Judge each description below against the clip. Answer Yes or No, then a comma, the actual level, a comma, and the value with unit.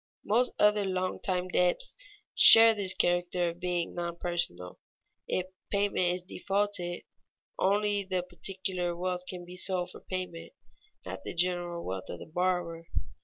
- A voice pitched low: No, medium, 180 Hz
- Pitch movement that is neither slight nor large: No, narrow, 1.5 semitones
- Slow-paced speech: No, average, 145 wpm